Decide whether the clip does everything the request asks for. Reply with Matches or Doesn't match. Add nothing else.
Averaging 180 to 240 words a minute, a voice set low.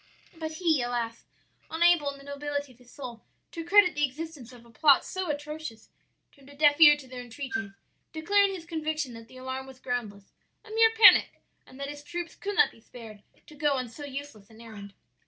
Doesn't match